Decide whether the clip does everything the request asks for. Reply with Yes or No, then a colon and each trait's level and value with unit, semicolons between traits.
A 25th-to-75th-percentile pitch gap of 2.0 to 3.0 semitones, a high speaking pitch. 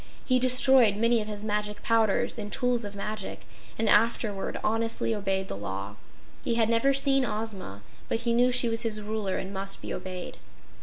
Yes: narrow, 2.6 semitones; high, 215 Hz